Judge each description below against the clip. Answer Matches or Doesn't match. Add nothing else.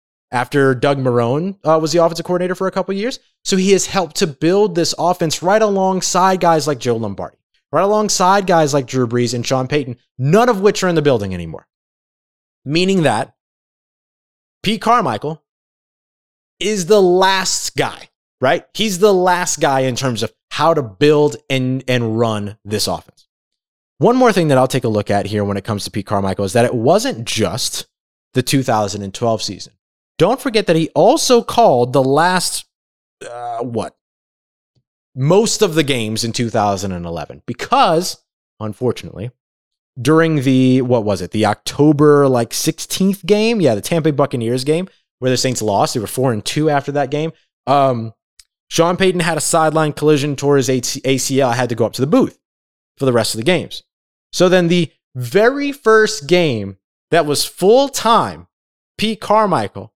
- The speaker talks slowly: Doesn't match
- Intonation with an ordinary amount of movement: Doesn't match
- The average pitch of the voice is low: Doesn't match